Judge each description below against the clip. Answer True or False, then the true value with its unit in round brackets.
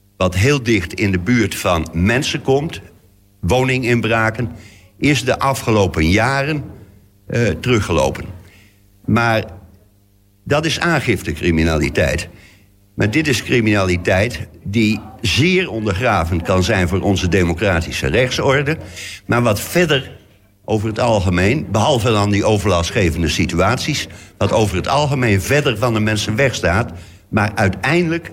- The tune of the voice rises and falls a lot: False (4.2 semitones)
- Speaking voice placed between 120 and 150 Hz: False (105 Hz)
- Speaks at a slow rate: True (115 wpm)